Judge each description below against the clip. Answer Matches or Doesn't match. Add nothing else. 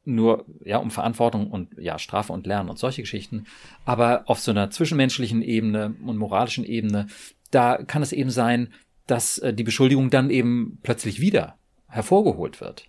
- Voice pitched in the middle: Doesn't match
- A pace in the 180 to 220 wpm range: Doesn't match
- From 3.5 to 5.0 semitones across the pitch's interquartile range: Doesn't match